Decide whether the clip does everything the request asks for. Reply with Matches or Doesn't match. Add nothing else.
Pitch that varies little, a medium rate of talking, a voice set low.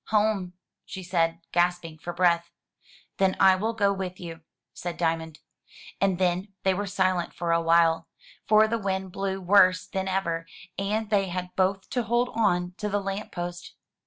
Doesn't match